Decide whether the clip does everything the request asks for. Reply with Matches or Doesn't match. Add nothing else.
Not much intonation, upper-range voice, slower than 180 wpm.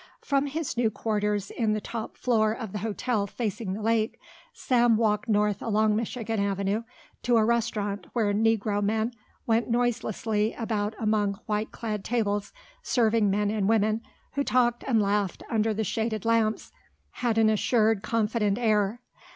Matches